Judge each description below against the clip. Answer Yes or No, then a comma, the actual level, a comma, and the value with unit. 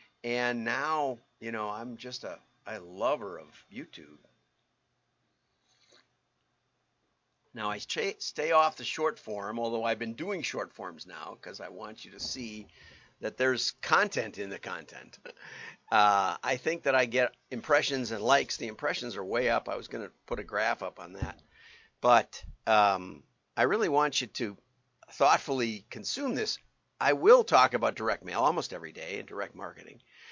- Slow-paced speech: No, average, 165 wpm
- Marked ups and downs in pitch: No, average, 4.8 semitones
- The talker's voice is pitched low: Yes, low, 125 Hz